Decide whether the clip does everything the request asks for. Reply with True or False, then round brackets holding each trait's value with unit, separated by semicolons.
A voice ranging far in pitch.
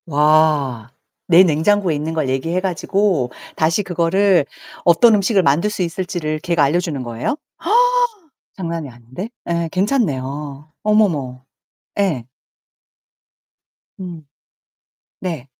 False (4.6 semitones)